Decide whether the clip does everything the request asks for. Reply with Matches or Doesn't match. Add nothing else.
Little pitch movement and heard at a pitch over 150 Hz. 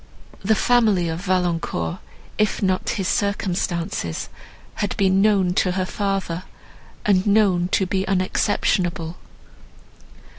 Matches